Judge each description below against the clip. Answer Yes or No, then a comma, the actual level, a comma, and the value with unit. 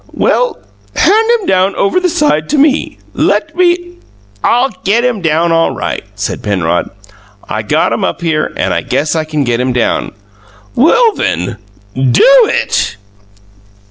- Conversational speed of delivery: Yes, average, 160 wpm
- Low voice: No, high, 195 Hz